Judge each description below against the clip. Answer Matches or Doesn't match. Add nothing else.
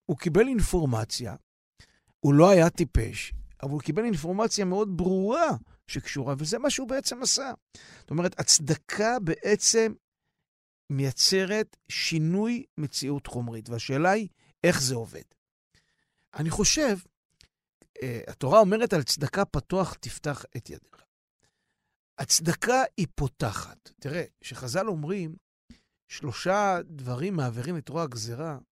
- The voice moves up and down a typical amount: Doesn't match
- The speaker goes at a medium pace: Matches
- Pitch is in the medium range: Matches